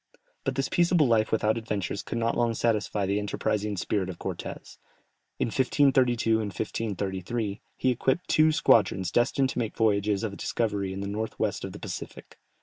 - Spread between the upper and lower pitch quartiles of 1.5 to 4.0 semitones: Yes, average, 2.9 semitones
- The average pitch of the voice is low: Yes, low, 110 Hz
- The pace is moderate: Yes, average, 170 wpm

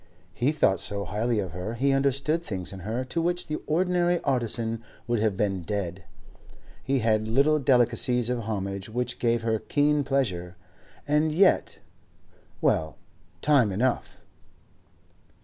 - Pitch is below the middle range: Yes, low, 120 Hz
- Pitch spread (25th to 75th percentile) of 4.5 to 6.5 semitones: Yes, average, 5.2 semitones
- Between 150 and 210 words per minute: No, slow, 135 wpm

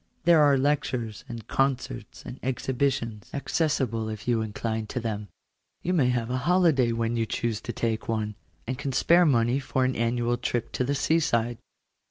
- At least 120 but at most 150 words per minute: No, average, 180 wpm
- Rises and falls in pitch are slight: No, average, 3.3 semitones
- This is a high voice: No, low, 120 Hz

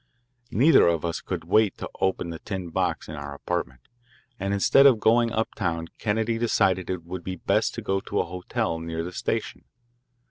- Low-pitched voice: Yes, very low, 95 Hz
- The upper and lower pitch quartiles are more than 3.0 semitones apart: Yes, average, 4.7 semitones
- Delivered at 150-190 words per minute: Yes, average, 185 wpm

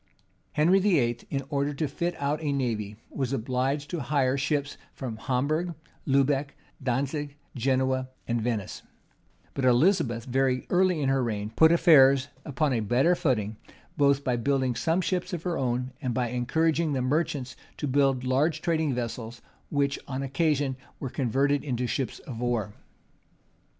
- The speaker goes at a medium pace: Yes, average, 155 wpm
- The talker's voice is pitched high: No, low, 135 Hz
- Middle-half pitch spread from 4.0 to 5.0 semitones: No, average, 3.1 semitones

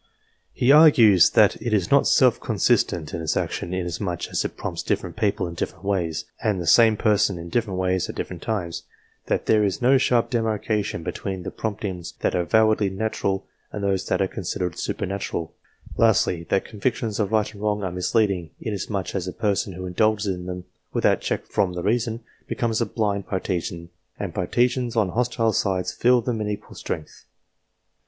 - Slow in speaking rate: No, average, 185 wpm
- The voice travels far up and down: No, average, 3.3 semitones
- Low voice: Yes, low, 100 Hz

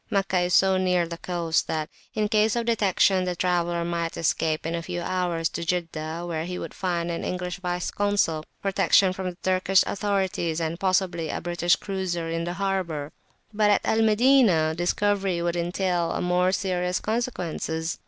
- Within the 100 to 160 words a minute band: No, average, 175 wpm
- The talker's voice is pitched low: No, medium, 180 Hz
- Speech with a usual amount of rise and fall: No, narrow, 2.3 semitones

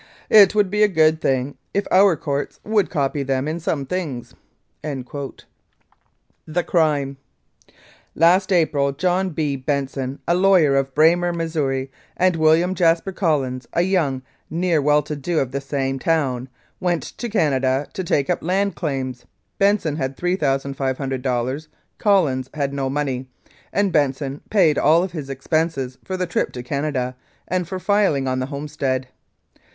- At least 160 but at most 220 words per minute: No, average, 150 wpm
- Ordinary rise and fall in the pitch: Yes, average, 4.6 semitones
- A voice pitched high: No, medium, 150 Hz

